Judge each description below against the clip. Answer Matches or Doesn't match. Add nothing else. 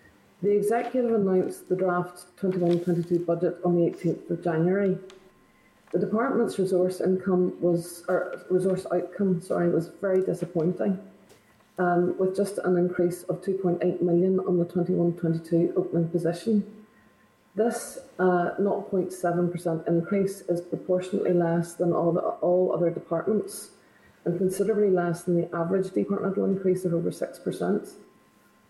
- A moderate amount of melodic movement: Doesn't match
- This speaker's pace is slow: Matches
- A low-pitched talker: Doesn't match